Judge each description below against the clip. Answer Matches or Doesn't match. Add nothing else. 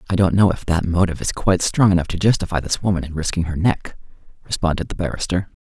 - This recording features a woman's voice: Doesn't match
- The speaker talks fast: Matches